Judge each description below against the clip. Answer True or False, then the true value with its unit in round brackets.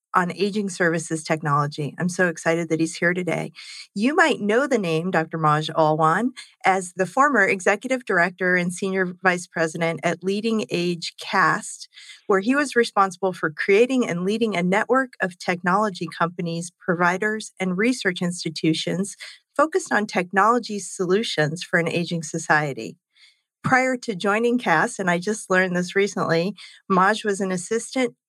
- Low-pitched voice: False (185 Hz)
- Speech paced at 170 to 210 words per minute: False (150 wpm)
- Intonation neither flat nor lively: True (4.0 semitones)